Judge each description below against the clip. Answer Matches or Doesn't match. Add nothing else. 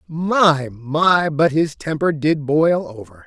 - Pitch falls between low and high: Matches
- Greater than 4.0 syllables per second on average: Doesn't match